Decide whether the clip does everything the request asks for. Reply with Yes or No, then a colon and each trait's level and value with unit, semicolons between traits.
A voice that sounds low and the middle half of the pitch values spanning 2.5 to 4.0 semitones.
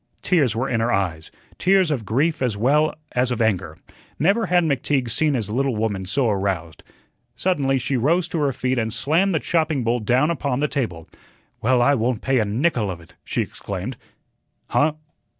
No: low, 125 Hz; average, 5.3 semitones